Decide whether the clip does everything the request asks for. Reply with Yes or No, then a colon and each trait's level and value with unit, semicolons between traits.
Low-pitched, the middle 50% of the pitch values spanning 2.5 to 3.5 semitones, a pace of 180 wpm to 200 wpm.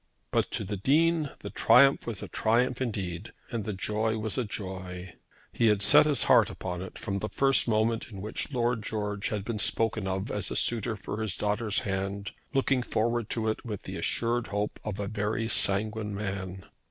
Yes: low, 110 Hz; average, 2.9 semitones; average, 195 wpm